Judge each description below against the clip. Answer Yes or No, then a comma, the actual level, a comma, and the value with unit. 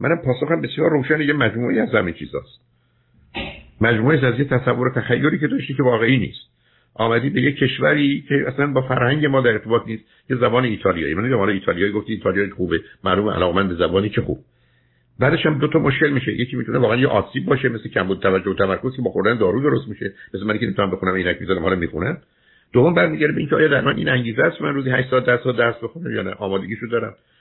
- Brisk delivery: Yes, fast, 220 wpm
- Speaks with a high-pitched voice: No, low, 120 Hz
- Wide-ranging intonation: Yes, wide, 5.7 semitones